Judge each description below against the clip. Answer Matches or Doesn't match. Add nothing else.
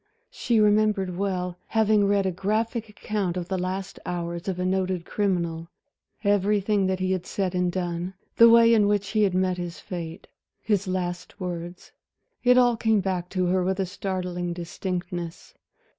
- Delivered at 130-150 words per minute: Doesn't match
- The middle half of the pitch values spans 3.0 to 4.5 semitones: Doesn't match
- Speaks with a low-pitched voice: Doesn't match